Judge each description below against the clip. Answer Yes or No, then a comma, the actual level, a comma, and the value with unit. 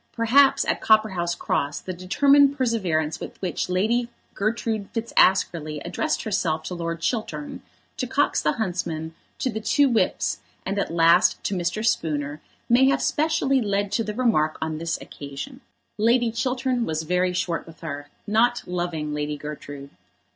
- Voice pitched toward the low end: No, high, 190 Hz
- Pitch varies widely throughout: Yes, wide, 6.5 semitones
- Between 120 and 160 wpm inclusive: Yes, average, 155 wpm